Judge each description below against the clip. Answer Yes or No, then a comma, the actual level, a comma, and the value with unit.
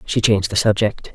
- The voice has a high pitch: No, low, 105 Hz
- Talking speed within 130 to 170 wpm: No, fast, 210 wpm